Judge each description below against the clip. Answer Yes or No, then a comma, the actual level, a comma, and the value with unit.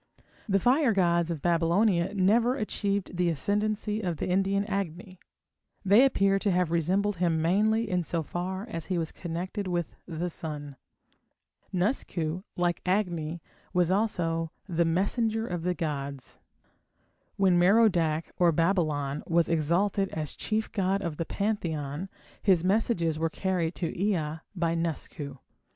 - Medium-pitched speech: Yes, medium, 180 Hz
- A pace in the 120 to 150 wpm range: Yes, average, 140 wpm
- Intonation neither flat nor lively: Yes, average, 3.3 semitones